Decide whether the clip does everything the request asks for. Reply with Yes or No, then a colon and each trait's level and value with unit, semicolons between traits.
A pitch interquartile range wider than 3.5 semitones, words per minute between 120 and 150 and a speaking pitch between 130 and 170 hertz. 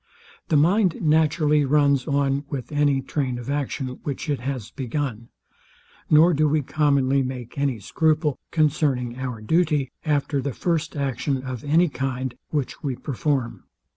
No: narrow, 2.6 semitones; average, 145 wpm; medium, 140 Hz